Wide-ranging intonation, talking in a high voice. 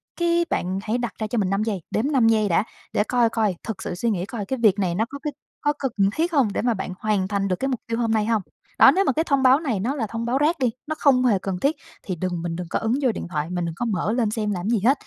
No: average, 4.9 semitones; high, 225 Hz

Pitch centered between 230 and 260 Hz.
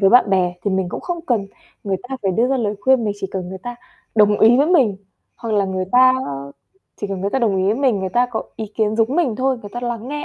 No: high, 220 Hz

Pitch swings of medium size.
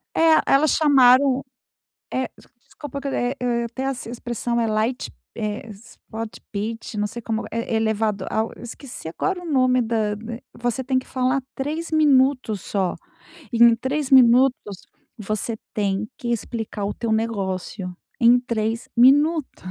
Yes: average, 3.2 semitones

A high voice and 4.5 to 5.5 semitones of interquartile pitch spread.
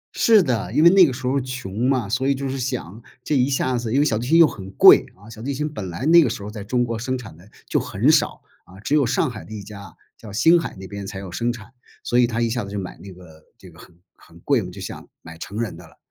No: low, 115 Hz; average, 4.9 semitones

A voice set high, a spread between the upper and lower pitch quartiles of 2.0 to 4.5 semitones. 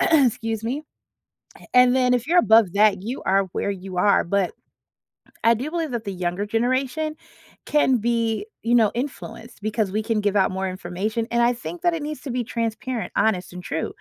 Yes: high, 225 Hz; average, 3.9 semitones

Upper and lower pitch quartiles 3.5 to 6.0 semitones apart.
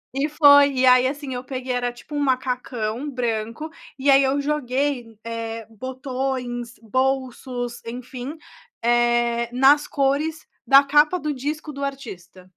No: average, 2.8 semitones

